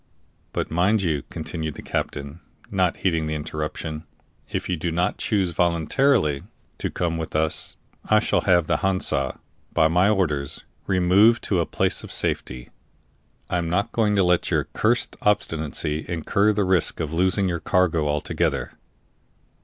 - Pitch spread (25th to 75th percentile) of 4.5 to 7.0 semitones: No, average, 3.5 semitones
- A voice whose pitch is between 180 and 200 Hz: No, very low, 85 Hz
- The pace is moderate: Yes, average, 155 wpm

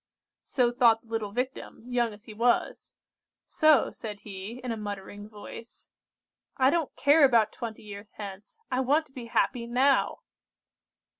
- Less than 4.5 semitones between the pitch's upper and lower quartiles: Yes, average, 3.4 semitones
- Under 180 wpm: Yes, average, 155 wpm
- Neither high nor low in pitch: No, high, 235 Hz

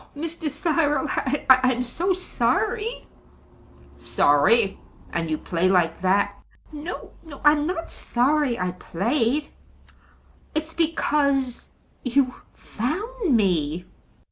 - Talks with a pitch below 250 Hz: No, very high, 275 Hz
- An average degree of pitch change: No, wide, 8.1 semitones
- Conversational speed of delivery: No, slow, 100 wpm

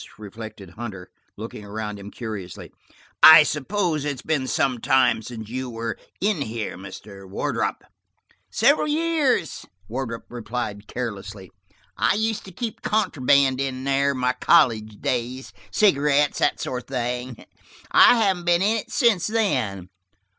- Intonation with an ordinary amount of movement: No, wide, 7.1 semitones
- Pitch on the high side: No, low, 130 Hz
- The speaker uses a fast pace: No, average, 140 wpm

